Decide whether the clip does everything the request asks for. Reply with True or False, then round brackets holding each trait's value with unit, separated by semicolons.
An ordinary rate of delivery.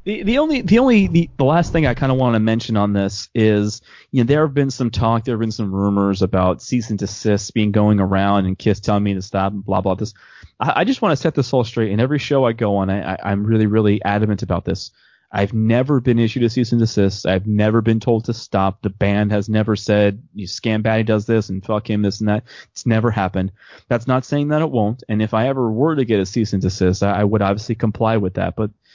False (265 wpm)